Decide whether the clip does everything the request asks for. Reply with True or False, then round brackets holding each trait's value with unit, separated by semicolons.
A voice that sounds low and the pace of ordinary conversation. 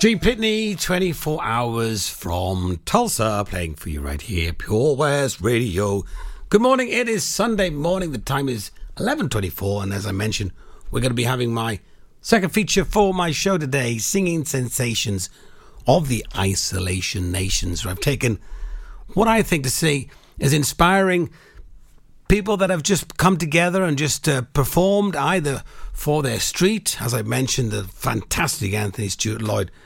True (130 Hz; 160 wpm)